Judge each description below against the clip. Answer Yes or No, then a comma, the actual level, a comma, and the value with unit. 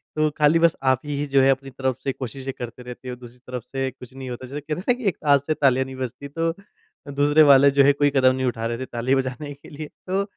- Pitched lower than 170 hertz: Yes, low, 135 Hz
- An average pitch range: No, narrow, 2.1 semitones